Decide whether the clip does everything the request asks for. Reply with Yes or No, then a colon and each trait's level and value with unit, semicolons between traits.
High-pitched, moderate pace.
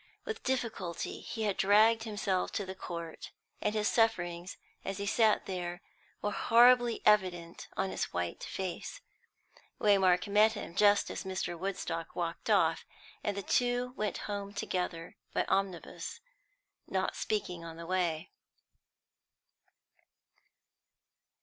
No: high, 195 Hz; slow, 125 wpm